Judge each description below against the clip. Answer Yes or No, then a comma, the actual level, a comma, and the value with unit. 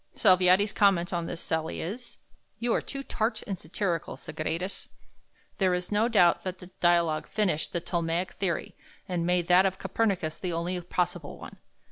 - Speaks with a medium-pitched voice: Yes, medium, 180 Hz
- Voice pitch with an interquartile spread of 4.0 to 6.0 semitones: No, narrow, 2.5 semitones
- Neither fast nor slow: Yes, average, 165 wpm